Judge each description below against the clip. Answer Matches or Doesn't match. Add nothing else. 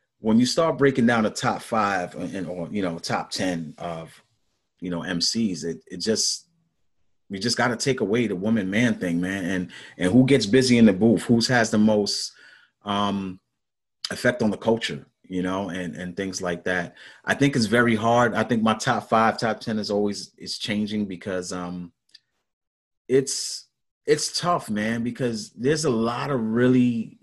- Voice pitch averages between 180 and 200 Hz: Doesn't match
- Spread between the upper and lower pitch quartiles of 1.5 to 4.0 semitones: Doesn't match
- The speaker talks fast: Doesn't match